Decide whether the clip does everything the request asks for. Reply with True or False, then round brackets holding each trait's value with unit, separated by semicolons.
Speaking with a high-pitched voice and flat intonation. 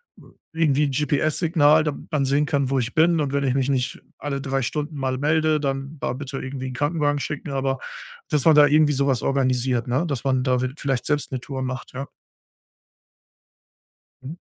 False (140 Hz; 2.2 semitones)